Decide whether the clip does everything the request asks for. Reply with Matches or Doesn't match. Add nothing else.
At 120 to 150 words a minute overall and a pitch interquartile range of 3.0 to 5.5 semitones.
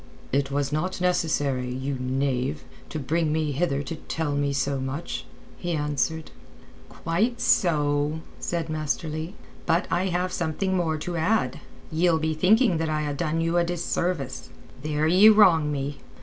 Doesn't match